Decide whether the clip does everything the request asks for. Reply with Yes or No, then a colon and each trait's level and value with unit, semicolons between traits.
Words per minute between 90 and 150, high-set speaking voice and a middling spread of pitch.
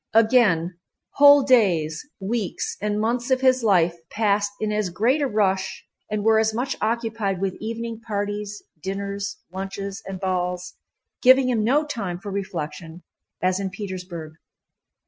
Yes: average, 145 wpm; high, 205 Hz; average, 3.3 semitones